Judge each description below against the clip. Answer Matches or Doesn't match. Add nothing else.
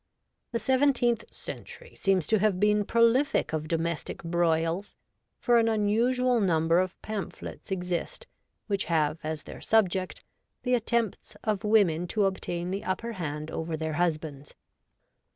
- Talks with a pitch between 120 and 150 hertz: Doesn't match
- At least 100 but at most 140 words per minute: Matches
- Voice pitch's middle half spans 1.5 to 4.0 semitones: Doesn't match